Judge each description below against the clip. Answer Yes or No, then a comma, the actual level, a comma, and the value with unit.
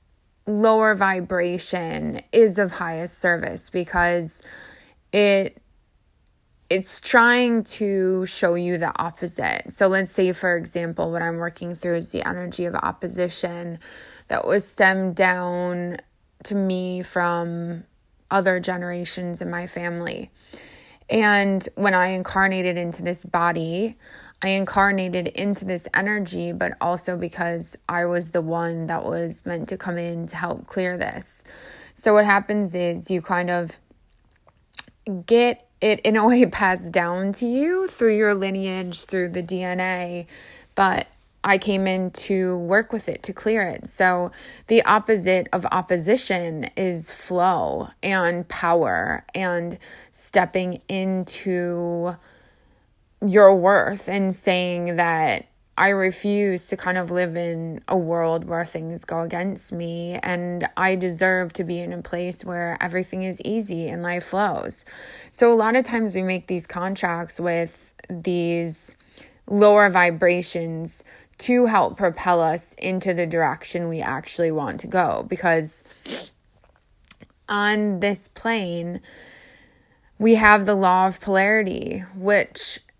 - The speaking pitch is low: No, medium, 180 Hz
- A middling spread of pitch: No, narrow, 2.3 semitones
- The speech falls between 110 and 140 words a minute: Yes, slow, 135 wpm